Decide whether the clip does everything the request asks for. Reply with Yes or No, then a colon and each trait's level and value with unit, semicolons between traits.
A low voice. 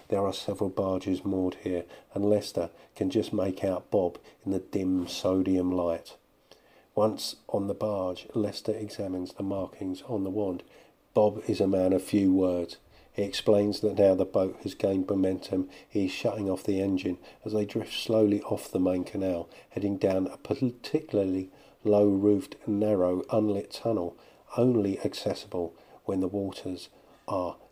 Yes: very low, 95 Hz